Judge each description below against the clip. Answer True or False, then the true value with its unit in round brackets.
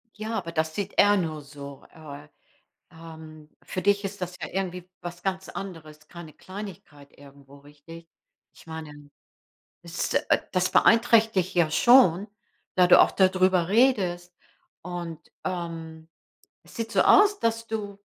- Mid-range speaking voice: True (175 Hz)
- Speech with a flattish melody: False (3.8 semitones)